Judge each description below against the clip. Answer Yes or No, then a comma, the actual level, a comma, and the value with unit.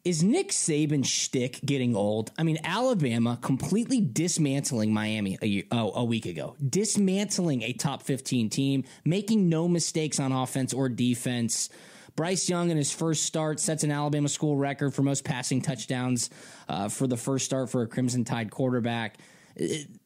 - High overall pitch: No, medium, 140 Hz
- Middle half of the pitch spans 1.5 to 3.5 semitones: No, average, 4.6 semitones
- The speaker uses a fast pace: No, average, 170 wpm